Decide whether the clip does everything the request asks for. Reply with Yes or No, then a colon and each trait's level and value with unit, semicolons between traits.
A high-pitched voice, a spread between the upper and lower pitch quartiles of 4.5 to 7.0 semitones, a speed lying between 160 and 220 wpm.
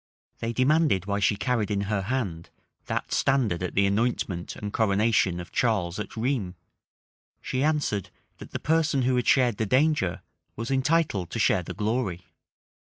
No: low, 110 Hz; average, 4.9 semitones; average, 165 wpm